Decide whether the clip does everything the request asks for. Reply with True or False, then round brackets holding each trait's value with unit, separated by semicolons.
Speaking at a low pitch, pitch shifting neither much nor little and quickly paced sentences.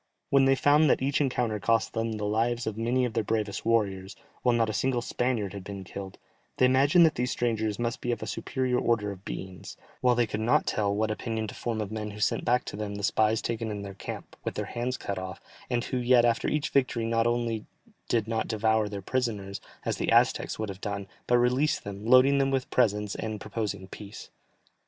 True (115 Hz; 3.0 semitones; 225 wpm)